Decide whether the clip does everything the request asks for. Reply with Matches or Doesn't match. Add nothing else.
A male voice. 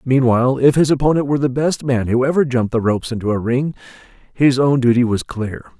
Matches